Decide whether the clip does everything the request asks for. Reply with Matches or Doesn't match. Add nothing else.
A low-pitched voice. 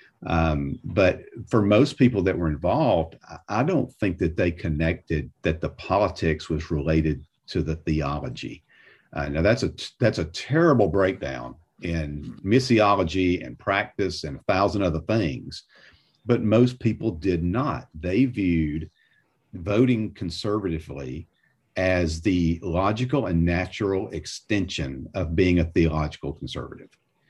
Matches